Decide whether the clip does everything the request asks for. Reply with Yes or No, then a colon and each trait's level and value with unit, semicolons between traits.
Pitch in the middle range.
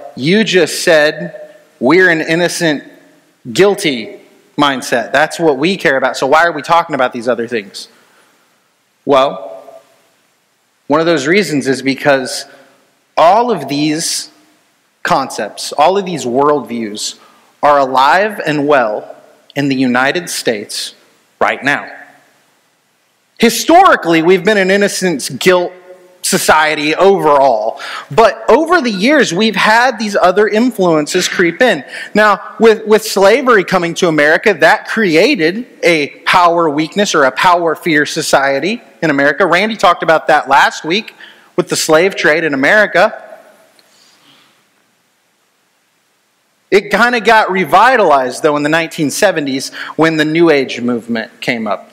Yes: medium, 170 Hz